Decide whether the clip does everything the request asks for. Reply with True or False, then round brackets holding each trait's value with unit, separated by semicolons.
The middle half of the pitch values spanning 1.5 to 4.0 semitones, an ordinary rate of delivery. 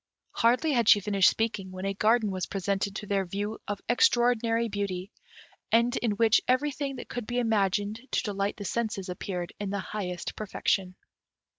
True (3.0 semitones; 170 wpm)